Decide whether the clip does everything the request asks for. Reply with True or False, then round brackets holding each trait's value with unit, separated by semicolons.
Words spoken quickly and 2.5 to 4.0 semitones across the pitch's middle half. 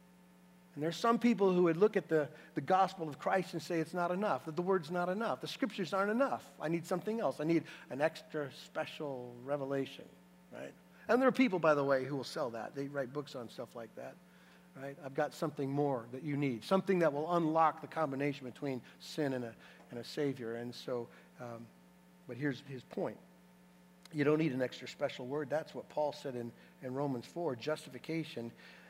False (210 wpm; 4.9 semitones)